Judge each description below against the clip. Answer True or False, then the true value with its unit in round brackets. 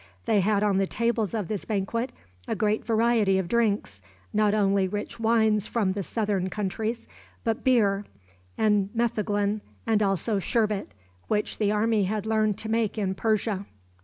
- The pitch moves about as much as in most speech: False (2.0 semitones)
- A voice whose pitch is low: False (210 Hz)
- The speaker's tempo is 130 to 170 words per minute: True (160 wpm)